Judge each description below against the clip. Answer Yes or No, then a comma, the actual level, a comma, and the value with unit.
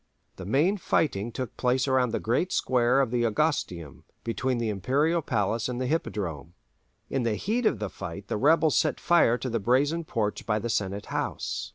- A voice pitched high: No, low, 120 Hz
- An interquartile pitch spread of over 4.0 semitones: Yes, average, 5.0 semitones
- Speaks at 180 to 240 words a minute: Yes, average, 190 wpm